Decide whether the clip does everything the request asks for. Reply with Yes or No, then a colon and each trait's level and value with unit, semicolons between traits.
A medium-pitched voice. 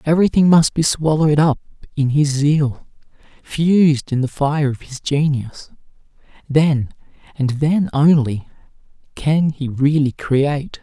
Yes: medium, 145 Hz